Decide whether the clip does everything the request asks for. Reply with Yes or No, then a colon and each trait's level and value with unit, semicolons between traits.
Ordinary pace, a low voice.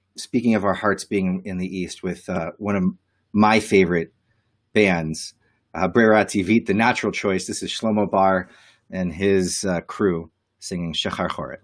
Yes: average, 165 wpm; low, 100 Hz